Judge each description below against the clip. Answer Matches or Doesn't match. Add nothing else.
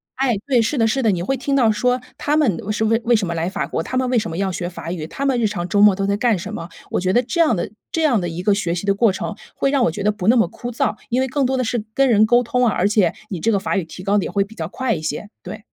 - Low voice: Doesn't match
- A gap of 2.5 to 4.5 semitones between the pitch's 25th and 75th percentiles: Doesn't match